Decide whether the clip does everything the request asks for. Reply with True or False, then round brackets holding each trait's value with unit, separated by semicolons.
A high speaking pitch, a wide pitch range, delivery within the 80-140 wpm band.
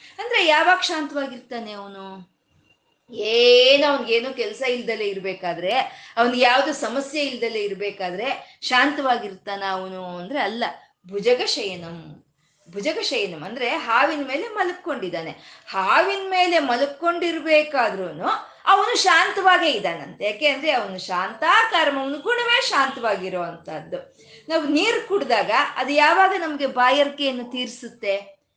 True (275 Hz; 9.0 semitones; 95 wpm)